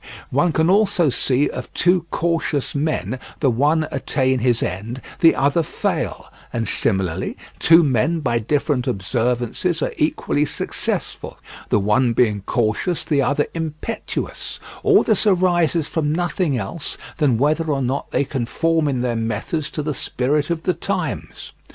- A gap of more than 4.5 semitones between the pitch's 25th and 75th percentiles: Yes, average, 5.0 semitones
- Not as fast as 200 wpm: Yes, average, 150 wpm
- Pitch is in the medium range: Yes, medium, 145 Hz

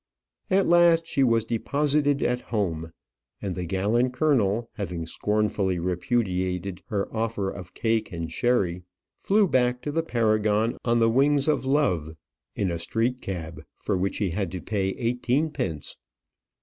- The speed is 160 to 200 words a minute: No, average, 150 wpm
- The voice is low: Yes, low, 110 Hz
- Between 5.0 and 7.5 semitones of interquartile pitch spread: Yes, wide, 5.4 semitones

